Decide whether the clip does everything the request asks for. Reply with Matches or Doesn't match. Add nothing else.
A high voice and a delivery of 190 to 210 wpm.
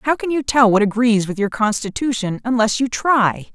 Matches